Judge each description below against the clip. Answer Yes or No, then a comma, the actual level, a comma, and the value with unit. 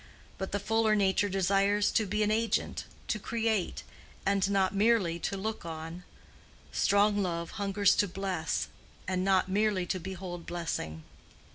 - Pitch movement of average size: No, narrow, 2.3 semitones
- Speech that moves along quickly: No, average, 145 wpm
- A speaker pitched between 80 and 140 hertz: No, high, 195 Hz